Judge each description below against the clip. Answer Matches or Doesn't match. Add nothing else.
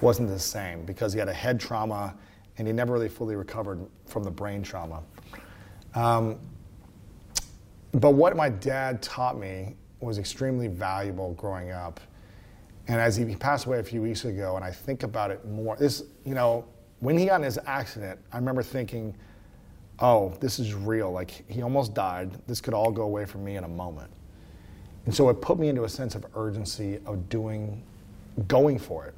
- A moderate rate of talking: Matches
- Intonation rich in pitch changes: Doesn't match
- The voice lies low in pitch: Matches